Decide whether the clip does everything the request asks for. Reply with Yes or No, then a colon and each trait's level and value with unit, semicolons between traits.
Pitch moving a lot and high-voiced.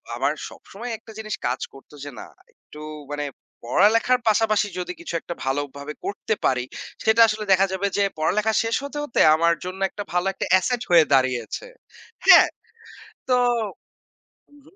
Yes: wide, 6.1 semitones; high, 195 Hz